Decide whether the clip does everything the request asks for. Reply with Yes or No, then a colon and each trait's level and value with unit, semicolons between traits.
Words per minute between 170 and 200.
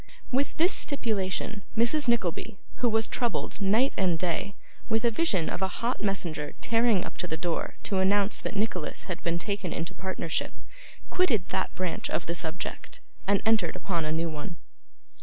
Yes: average, 175 wpm